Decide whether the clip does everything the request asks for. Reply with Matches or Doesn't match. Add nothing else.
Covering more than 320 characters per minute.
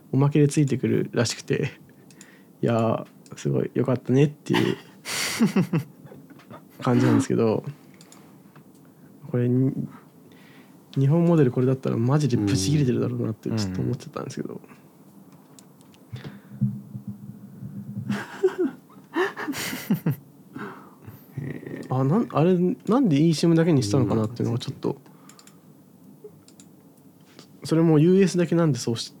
Doesn't match